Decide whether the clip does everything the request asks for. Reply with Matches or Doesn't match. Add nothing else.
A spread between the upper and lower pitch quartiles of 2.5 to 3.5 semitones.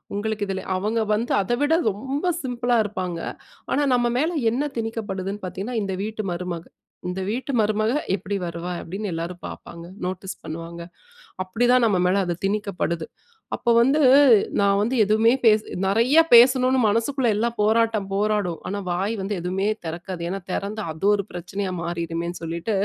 Doesn't match